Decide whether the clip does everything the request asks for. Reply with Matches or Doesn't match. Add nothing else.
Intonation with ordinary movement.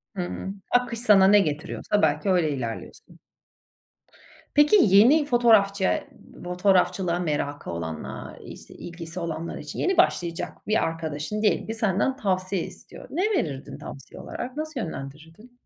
Doesn't match